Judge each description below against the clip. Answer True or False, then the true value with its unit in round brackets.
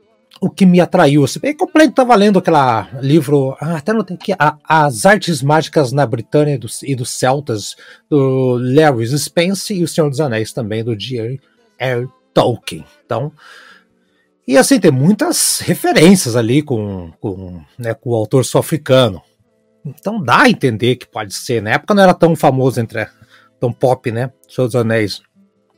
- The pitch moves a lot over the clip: True (6.3 semitones)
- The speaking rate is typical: True (170 wpm)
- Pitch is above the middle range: False (140 Hz)